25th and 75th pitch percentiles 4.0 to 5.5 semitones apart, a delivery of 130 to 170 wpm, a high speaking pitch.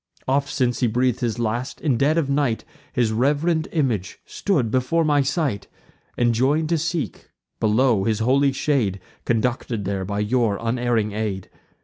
No: average, 4.4 semitones; average, 150 wpm; low, 125 Hz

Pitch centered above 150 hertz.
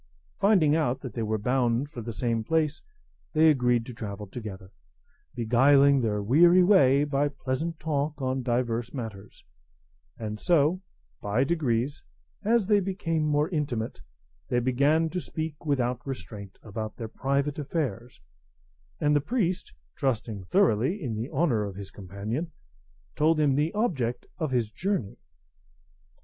No: low, 135 Hz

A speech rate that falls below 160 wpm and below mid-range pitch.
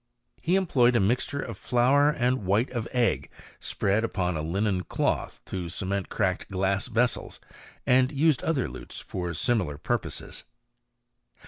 Yes: average, 145 wpm; low, 115 Hz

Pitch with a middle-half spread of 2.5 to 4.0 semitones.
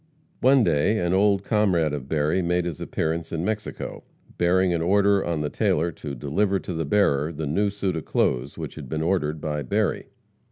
No: average, 4.4 semitones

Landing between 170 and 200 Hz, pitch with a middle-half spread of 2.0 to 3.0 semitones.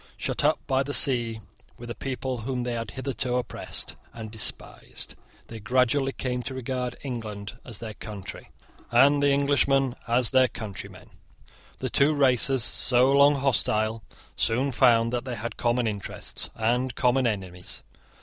No: low, 125 Hz; narrow, 2.6 semitones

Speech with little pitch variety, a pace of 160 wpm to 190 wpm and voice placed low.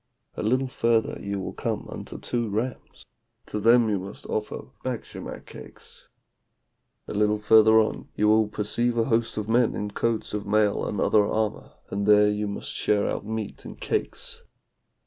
Yes: narrow, 1.4 semitones; average, 170 wpm; low, 105 Hz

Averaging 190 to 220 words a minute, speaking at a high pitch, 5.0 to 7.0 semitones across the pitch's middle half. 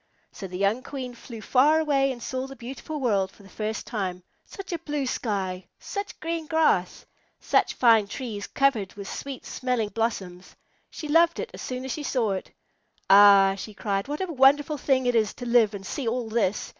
Yes: average, 200 wpm; high, 240 Hz; average, 5.3 semitones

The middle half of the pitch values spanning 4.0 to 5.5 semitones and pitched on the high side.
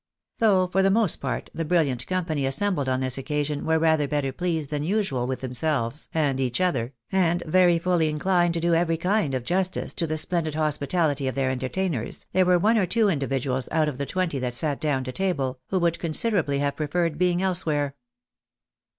No: average, 4.7 semitones; medium, 155 Hz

